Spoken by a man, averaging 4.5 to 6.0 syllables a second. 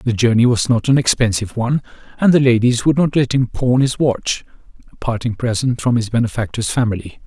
Yes: male; 5.8 syllables/s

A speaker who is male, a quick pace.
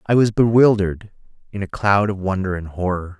No: male; average, 190 wpm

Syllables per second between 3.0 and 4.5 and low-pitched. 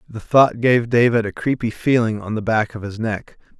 No: 5.0 syllables/s; low, 115 Hz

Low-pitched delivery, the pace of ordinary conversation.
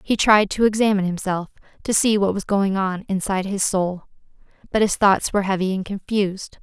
No: high, 195 Hz; average, 190 wpm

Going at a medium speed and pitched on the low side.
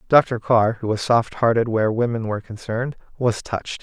Yes: average, 190 wpm; low, 115 Hz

